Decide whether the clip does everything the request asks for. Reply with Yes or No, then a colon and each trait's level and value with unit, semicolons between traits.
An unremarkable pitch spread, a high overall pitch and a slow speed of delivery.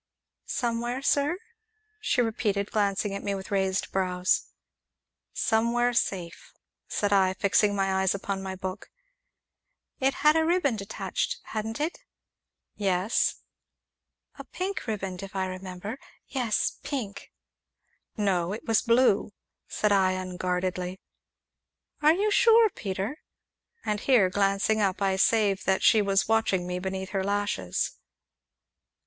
Yes: average, 3.4 semitones; high, 200 Hz; slow, 125 wpm